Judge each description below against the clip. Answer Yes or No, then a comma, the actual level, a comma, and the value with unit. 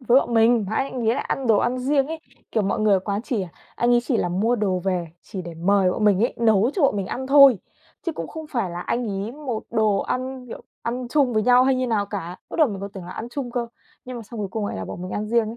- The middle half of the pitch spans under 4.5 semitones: Yes, average, 4.1 semitones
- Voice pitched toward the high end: Yes, high, 225 Hz